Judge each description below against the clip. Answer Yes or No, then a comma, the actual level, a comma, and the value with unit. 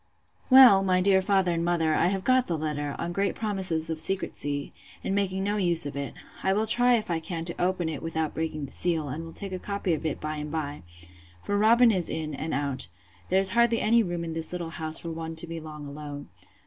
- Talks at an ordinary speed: No, fast, 235 wpm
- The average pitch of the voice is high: No, medium, 170 Hz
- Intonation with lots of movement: No, average, 3.7 semitones